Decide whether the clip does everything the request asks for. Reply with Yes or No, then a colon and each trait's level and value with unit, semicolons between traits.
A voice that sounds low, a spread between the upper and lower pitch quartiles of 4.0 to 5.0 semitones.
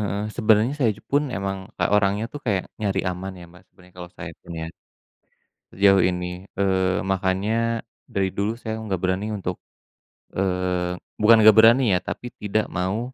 No: very low, 95 Hz; average, 2.7 semitones